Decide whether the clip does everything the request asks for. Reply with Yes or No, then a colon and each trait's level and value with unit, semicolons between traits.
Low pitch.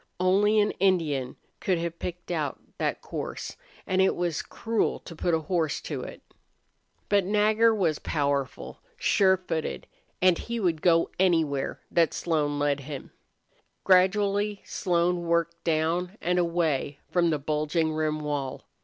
No: medium, 170 Hz